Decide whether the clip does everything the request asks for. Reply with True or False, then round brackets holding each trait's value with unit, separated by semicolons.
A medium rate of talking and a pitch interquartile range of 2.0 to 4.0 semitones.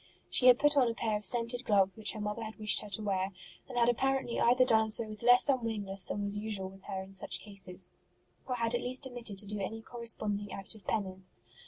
False (240 wpm; 3.2 semitones)